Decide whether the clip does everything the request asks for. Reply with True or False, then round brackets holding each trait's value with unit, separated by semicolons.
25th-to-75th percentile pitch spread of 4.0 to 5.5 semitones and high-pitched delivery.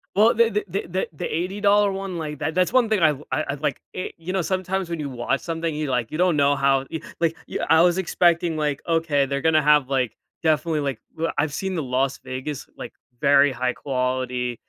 False (4.5 semitones; 155 Hz)